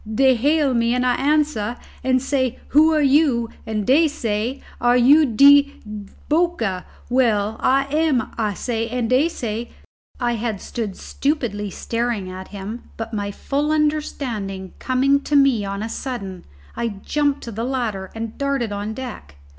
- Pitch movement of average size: Yes, average, 4.4 semitones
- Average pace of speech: Yes, average, 160 wpm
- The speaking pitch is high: Yes, high, 245 Hz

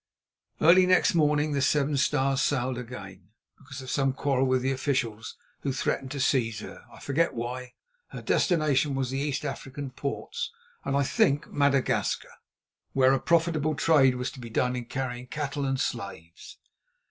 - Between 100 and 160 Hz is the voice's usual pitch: Yes, low, 135 Hz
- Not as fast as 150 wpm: No, average, 160 wpm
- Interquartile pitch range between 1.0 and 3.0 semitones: Yes, narrow, 2.5 semitones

